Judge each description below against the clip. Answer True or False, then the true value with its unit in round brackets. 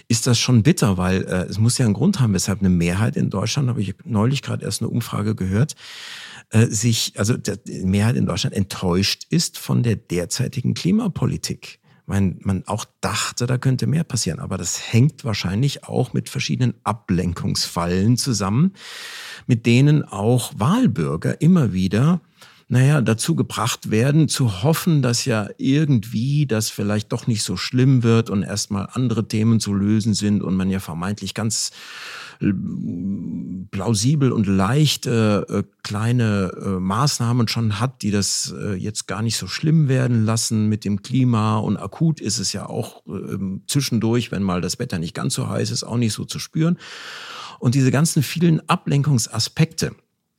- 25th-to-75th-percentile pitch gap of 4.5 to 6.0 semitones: True (4.8 semitones)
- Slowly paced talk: False (155 wpm)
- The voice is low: True (115 Hz)